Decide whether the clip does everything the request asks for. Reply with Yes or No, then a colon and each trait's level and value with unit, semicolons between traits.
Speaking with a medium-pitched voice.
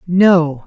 Yes: medium, 170 Hz